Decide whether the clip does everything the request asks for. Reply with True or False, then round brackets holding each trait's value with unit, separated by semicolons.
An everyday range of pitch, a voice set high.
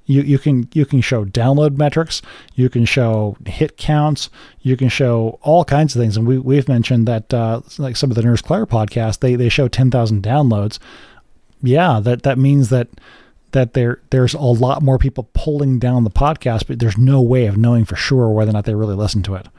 False (3.2 semitones; 125 Hz)